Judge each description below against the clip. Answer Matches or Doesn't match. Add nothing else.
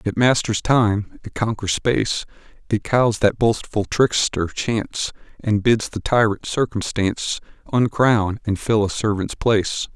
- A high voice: Doesn't match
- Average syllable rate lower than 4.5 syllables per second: Matches